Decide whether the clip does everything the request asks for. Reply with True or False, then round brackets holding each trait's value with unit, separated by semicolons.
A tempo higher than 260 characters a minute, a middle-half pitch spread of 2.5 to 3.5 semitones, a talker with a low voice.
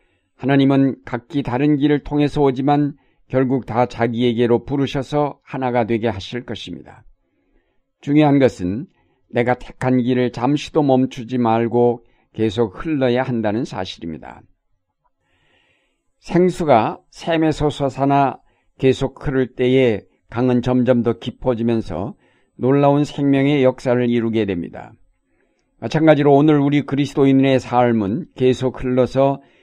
True (270 characters per minute; 2.8 semitones; 130 Hz)